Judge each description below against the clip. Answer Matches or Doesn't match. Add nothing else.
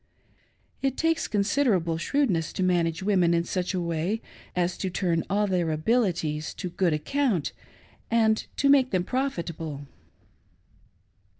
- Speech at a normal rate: Doesn't match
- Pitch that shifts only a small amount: Doesn't match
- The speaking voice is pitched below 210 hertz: Matches